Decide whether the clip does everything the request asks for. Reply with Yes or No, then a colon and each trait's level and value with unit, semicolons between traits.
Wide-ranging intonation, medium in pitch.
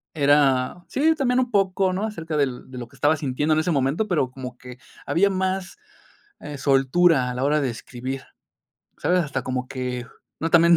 Yes: wide, 5.8 semitones; medium, 150 Hz